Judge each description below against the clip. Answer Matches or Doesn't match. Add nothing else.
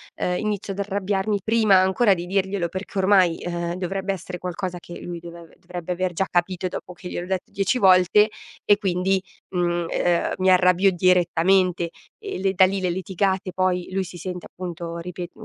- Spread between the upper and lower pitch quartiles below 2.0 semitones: Matches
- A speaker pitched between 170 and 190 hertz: Matches